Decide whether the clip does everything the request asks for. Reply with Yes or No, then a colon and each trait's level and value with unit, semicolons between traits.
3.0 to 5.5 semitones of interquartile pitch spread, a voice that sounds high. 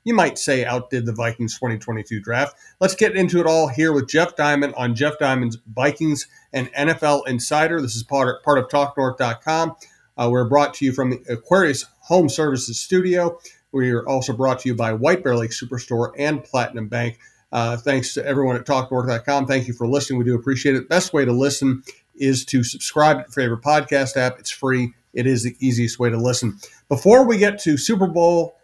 No: average, 3.5 semitones; low, 135 Hz